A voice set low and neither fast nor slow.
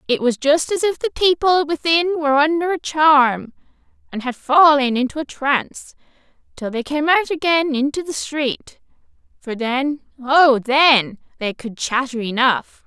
No: very high, 285 Hz; average, 150 wpm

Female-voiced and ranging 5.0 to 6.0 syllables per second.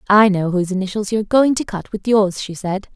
No: female; 6.3 syllables/s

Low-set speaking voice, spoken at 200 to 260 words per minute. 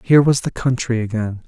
Yes: low, 120 Hz; fast, 205 wpm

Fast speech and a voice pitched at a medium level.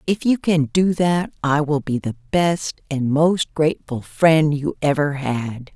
No: average, 175 wpm; medium, 150 Hz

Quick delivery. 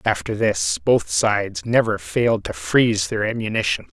No: average, 150 wpm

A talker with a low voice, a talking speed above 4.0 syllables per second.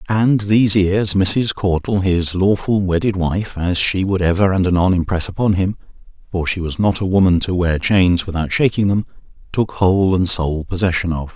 Yes: very low, 95 Hz; 5.0 syllables/s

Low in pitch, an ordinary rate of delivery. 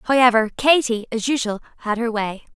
No: high, 235 Hz; average, 165 wpm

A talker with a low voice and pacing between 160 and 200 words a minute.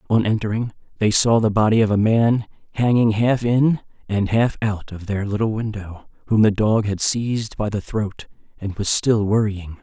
Yes: low, 110 Hz; average, 190 wpm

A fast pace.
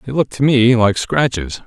Yes: fast, 215 wpm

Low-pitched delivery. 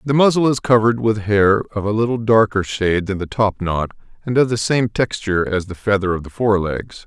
Yes: low, 105 Hz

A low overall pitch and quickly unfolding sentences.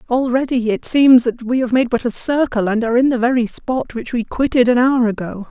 No: high, 245 Hz; fast, 240 wpm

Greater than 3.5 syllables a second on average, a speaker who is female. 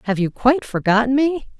Yes: 5.8 syllables/s; female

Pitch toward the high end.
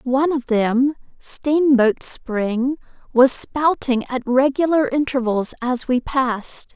Yes: very high, 260 Hz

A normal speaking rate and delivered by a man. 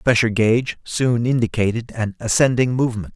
Yes: average, 150 wpm; male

